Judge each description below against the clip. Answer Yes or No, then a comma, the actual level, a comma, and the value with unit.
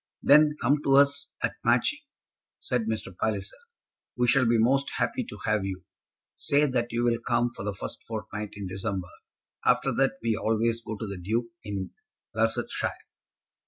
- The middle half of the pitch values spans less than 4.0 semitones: Yes, average, 3.5 semitones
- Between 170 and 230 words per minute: No, average, 160 wpm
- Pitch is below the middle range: Yes, low, 115 Hz